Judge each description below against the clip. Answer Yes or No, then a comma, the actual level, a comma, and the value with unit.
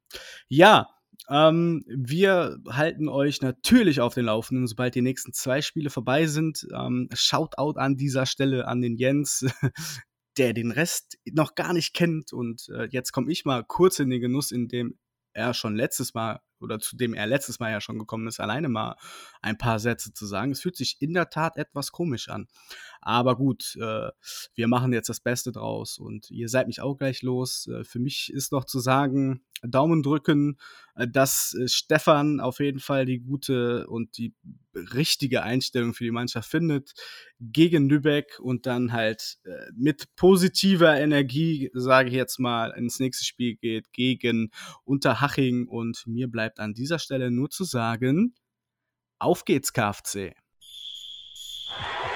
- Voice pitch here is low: Yes, low, 130 Hz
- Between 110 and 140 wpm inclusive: No, average, 160 wpm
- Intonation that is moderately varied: Yes, average, 3.3 semitones